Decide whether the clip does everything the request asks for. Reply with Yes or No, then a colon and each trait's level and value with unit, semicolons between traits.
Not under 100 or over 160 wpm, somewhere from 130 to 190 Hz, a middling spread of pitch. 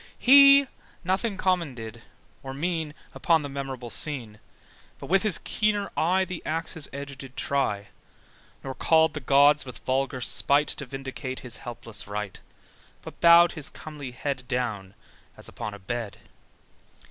Yes: average, 145 wpm; medium, 140 Hz; average, 5.0 semitones